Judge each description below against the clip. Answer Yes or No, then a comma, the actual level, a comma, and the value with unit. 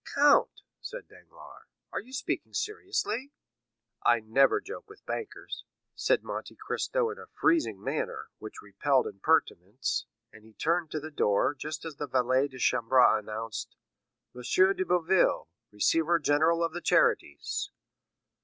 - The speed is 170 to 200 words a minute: No, average, 140 wpm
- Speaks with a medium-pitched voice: Yes, medium, 160 Hz